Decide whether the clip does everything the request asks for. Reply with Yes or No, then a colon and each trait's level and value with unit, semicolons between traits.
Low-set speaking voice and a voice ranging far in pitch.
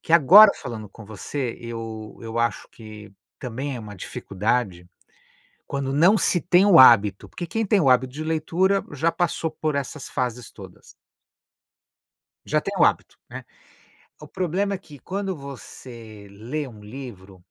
Yes: low, 130 Hz; wide, 6.7 semitones